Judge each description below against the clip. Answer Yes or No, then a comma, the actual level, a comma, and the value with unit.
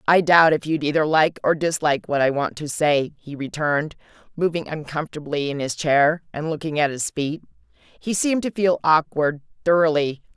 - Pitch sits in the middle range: Yes, medium, 155 Hz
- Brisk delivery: No, average, 175 wpm